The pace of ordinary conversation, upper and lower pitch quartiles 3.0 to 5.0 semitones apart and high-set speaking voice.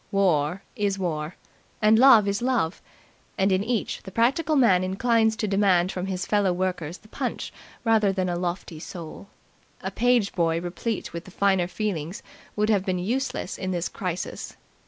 Yes: average, 170 wpm; average, 3.3 semitones; high, 195 Hz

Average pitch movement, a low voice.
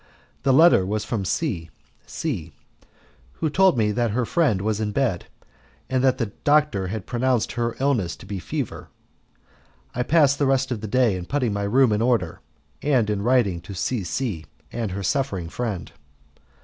Yes: average, 5.0 semitones; low, 115 Hz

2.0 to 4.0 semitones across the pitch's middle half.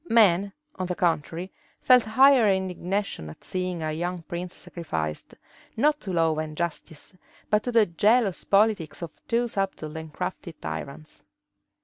No: average, 4.7 semitones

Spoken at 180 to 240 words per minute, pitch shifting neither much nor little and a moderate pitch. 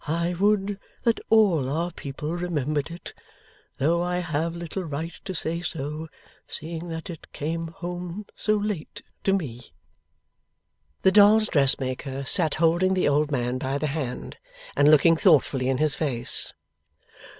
No: average, 145 wpm; average, 3.6 semitones; medium, 165 Hz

